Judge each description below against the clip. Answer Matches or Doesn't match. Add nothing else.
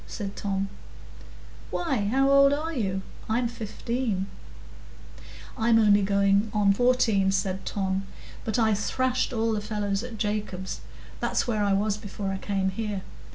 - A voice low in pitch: Doesn't match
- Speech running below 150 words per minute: Matches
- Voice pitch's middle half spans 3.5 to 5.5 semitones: Doesn't match